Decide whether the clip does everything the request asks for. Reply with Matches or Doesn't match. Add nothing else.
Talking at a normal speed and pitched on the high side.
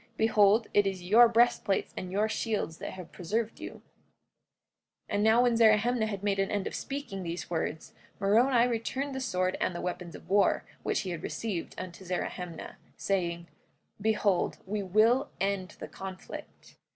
Matches